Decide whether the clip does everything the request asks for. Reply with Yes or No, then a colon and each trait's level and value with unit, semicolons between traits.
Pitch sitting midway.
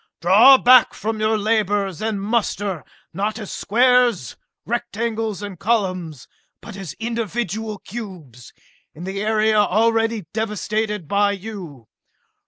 No: high, 210 Hz